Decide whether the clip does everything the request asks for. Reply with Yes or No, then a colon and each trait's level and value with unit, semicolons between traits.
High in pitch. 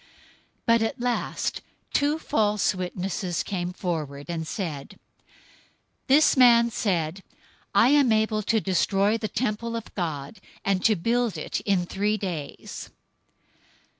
Yes: high, 205 Hz